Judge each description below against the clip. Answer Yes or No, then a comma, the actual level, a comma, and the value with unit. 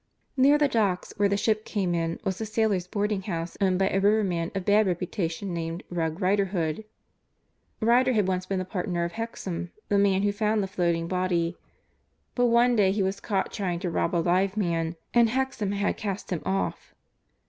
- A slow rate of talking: No, average, 190 wpm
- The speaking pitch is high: Yes, high, 195 Hz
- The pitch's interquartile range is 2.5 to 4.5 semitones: Yes, average, 3.2 semitones